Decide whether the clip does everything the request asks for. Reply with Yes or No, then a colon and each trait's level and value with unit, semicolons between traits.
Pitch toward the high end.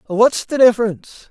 Yes: high, 225 Hz